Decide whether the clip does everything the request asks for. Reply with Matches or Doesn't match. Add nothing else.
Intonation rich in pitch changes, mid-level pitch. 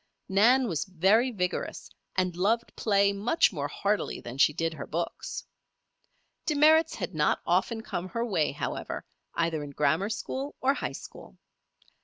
Doesn't match